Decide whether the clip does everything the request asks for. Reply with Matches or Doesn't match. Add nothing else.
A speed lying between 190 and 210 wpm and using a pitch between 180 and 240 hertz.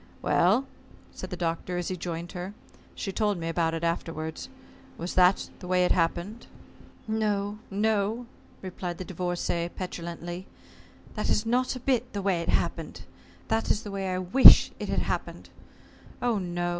Doesn't match